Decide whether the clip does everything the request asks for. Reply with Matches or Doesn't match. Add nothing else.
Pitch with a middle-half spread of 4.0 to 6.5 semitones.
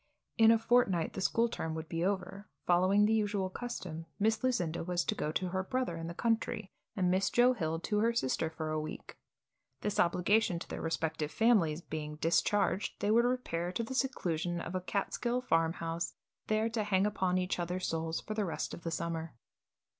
Matches